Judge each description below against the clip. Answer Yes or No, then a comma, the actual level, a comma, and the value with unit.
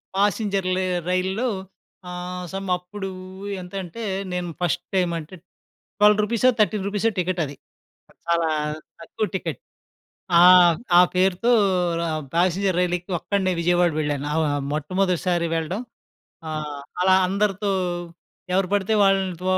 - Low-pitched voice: No, medium, 185 Hz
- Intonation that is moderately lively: No, narrow, 2.1 semitones